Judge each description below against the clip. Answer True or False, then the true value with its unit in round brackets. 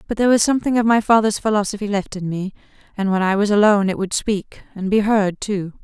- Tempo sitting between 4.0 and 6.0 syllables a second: False (6.2 syllables/s)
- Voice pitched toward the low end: False (205 Hz)